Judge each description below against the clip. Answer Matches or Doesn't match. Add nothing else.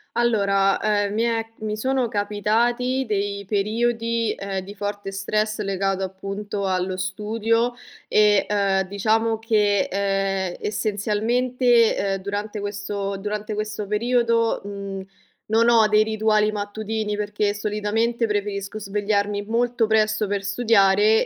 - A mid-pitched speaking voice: Doesn't match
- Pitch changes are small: Matches